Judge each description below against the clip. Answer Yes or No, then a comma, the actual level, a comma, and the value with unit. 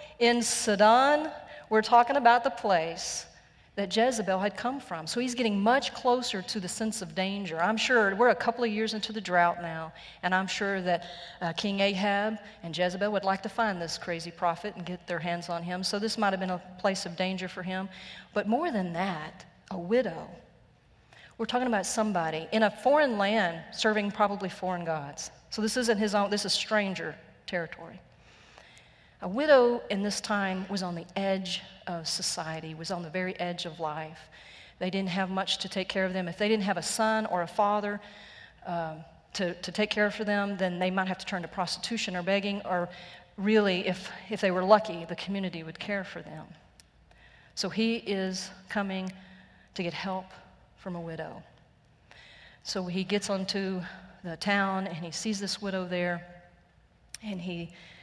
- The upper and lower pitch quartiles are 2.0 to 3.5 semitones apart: Yes, average, 3.1 semitones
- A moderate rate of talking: Yes, average, 190 wpm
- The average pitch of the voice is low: No, high, 190 Hz